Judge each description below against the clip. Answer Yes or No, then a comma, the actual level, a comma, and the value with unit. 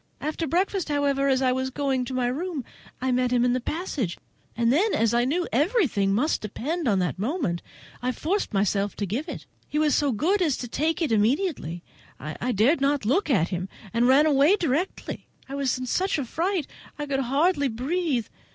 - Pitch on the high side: Yes, very high, 270 Hz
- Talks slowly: No, fast, 205 wpm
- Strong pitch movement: No, average, 4.8 semitones